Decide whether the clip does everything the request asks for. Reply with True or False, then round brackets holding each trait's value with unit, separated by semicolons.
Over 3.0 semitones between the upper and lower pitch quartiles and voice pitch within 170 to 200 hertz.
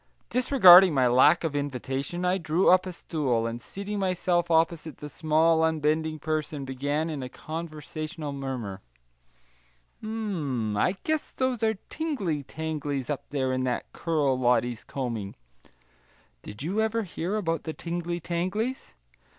False (4.7 semitones; 160 Hz)